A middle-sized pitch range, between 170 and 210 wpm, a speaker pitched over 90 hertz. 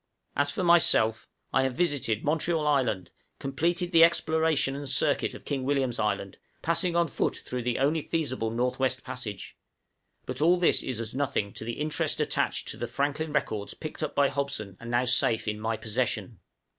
Yes: average, 4.9 semitones; average, 180 wpm; low, 135 Hz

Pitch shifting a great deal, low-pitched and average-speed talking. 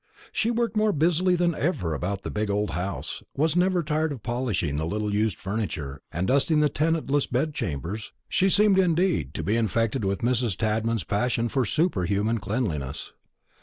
Yes: wide, 8.1 semitones; low, 115 Hz; average, 170 wpm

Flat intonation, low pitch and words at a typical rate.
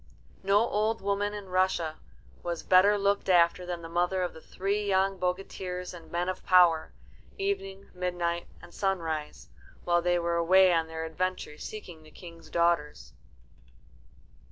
No: narrow, 2.3 semitones; medium, 180 Hz; average, 150 wpm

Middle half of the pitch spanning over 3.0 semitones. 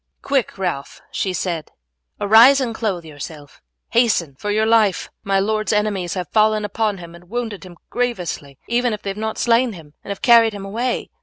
Yes: average, 4.2 semitones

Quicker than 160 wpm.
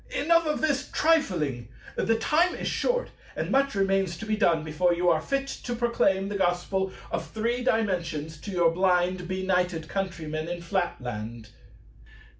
No: average, 155 wpm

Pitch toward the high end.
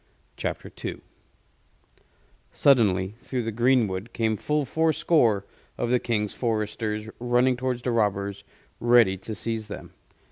No: low, 115 Hz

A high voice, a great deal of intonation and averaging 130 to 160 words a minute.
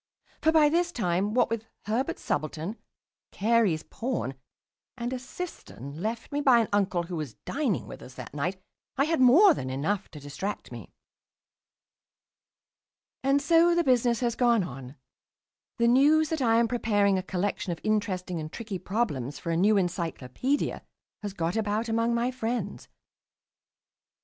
Yes: high, 220 Hz; wide, 6.2 semitones; average, 155 wpm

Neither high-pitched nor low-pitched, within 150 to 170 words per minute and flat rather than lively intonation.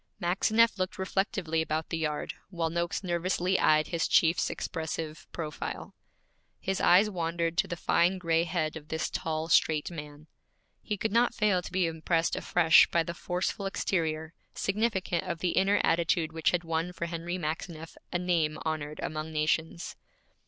Yes: medium, 170 Hz; average, 160 wpm; narrow, 2.3 semitones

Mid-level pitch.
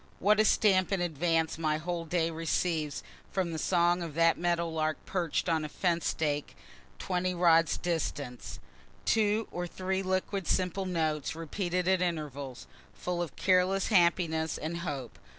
Yes: medium, 170 Hz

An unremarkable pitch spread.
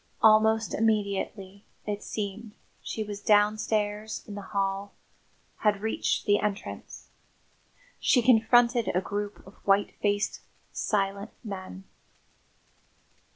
No: narrow, 1.5 semitones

